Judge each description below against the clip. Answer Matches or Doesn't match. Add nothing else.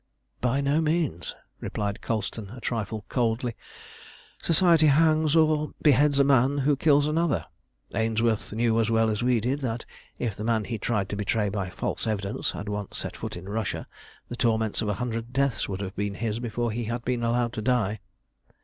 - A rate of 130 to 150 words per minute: Doesn't match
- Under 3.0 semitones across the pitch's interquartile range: Doesn't match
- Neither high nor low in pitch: Doesn't match